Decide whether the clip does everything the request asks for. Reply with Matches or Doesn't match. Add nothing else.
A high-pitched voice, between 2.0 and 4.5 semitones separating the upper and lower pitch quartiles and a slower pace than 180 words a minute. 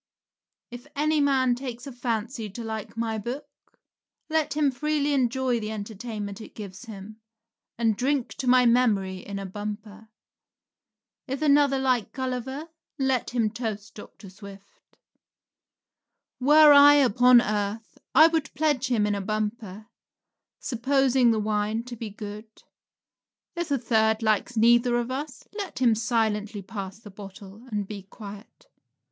Matches